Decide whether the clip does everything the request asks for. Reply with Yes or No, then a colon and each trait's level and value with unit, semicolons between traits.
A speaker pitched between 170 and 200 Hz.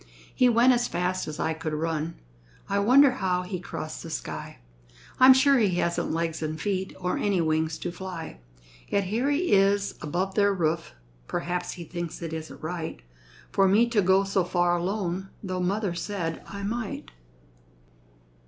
Yes: medium, 185 Hz